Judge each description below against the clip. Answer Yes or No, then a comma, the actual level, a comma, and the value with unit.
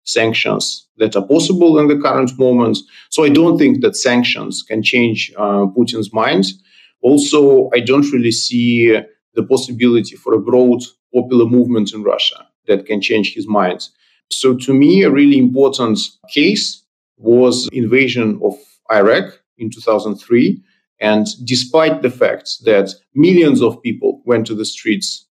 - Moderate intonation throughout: Yes, average, 4.5 semitones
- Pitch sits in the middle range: No, low, 125 Hz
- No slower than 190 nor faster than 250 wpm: No, average, 150 wpm